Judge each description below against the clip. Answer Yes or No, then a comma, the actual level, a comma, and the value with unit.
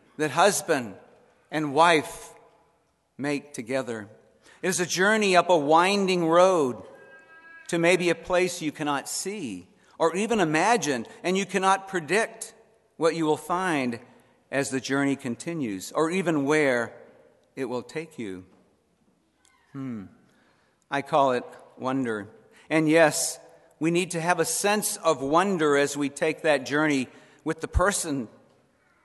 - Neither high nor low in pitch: Yes, medium, 165 Hz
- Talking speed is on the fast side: No, slow, 135 wpm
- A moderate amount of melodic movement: Yes, average, 4.3 semitones